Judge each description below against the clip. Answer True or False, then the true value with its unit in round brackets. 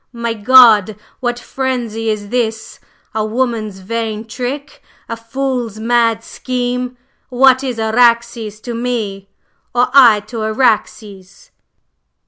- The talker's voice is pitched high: True (230 Hz)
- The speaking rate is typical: False (110 wpm)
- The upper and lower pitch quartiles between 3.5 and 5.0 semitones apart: False (2.4 semitones)